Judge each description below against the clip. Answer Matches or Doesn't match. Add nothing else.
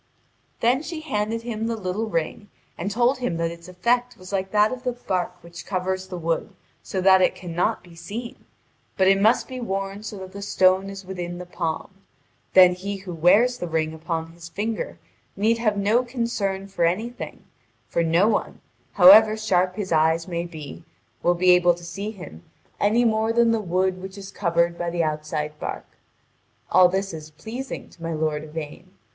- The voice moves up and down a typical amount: Matches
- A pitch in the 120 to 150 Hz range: Doesn't match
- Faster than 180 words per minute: Matches